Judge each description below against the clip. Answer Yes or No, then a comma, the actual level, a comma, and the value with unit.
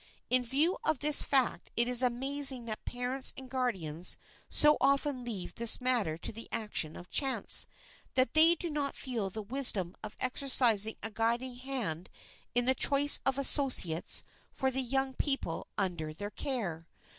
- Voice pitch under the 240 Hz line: No, very high, 250 Hz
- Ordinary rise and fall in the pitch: Yes, average, 4.2 semitones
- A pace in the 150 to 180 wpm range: Yes, average, 160 wpm